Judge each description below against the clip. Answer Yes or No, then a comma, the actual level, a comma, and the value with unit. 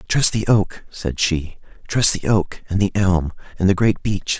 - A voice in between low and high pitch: No, very low, 95 Hz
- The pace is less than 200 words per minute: No, fast, 205 wpm